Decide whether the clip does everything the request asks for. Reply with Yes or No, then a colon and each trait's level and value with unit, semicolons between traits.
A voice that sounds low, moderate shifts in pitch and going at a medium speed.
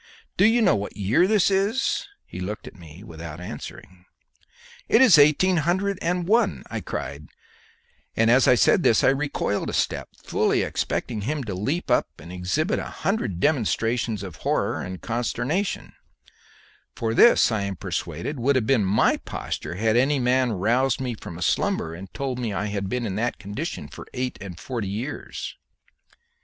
No: low, 120 Hz; wide, 7.3 semitones; average, 175 wpm